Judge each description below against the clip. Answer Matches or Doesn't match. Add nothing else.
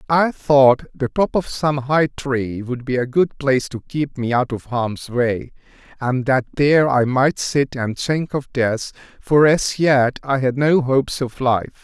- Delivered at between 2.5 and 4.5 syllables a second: Matches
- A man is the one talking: Matches